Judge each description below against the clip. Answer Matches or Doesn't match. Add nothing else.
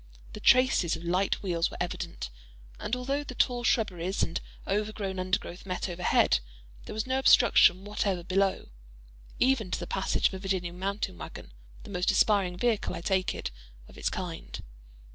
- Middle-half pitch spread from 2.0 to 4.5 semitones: Matches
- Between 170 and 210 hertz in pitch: Matches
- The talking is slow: Doesn't match